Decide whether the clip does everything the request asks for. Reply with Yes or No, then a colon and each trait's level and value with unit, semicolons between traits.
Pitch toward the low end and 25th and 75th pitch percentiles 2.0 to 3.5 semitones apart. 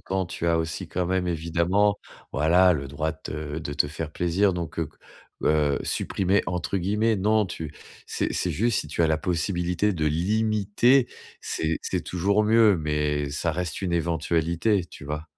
No: very low, 85 Hz; average, 3.9 semitones